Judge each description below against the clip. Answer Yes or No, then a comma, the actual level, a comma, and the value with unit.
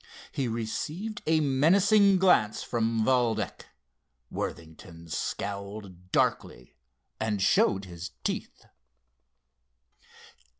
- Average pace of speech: No, slow, 80 wpm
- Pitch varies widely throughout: Yes, wide, 8.0 semitones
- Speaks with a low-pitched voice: Yes, low, 110 Hz